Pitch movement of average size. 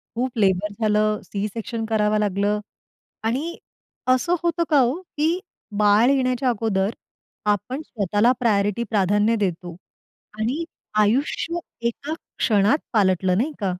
Yes: average, 3.9 semitones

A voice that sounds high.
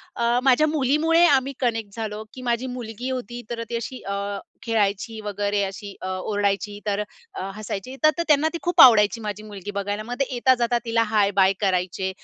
Yes: high, 225 Hz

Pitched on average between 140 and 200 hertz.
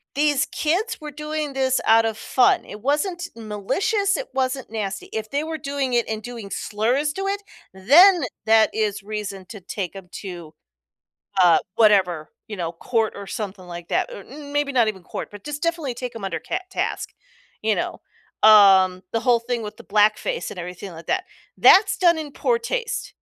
No: high, 230 Hz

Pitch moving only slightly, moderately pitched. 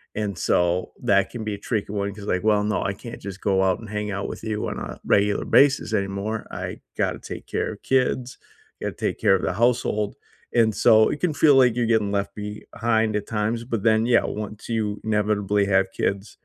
No: narrow, 2.2 semitones; low, 105 Hz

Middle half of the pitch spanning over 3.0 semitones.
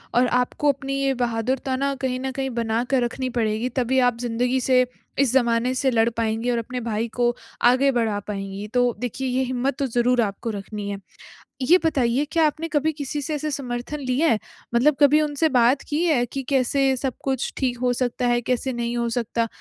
No: narrow, 2.5 semitones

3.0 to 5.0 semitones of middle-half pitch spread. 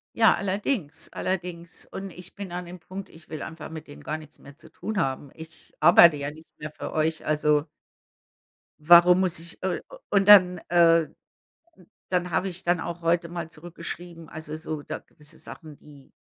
No: narrow, 2.5 semitones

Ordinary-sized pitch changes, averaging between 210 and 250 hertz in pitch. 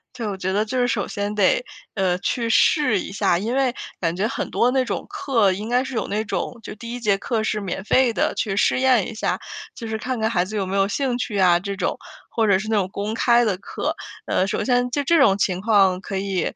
Yes: average, 3.8 semitones; high, 215 Hz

